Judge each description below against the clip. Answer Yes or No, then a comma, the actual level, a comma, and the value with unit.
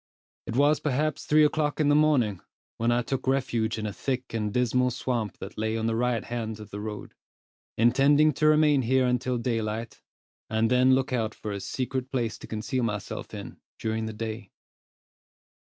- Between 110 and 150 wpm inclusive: No, average, 185 wpm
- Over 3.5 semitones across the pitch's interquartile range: No, average, 3.2 semitones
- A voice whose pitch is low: Yes, low, 120 Hz